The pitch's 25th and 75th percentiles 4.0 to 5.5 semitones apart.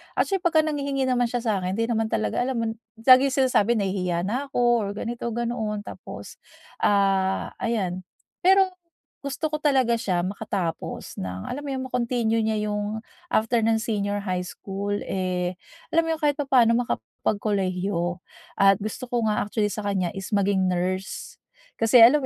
Yes: average, 4.3 semitones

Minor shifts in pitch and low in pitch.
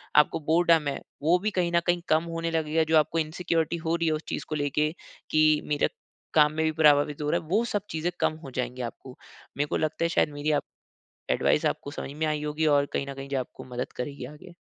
No: narrow, 2.1 semitones; medium, 155 Hz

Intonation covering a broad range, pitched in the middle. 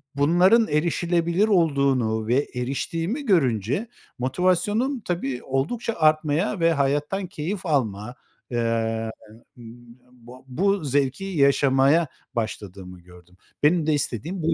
Yes: wide, 6.3 semitones; medium, 145 Hz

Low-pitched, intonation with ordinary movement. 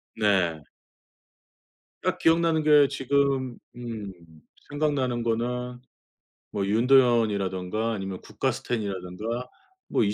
Yes: low, 115 Hz; average, 4.5 semitones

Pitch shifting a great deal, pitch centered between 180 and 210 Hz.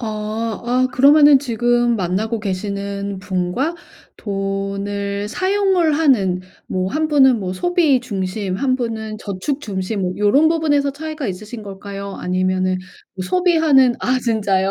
No: wide, 6.1 semitones; high, 220 Hz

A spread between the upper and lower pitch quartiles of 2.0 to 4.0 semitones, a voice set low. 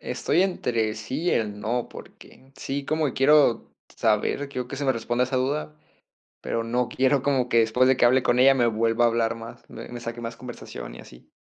Yes: average, 2.7 semitones; low, 125 Hz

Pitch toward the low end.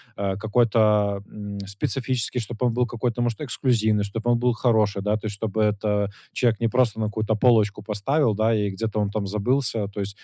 Yes: low, 110 Hz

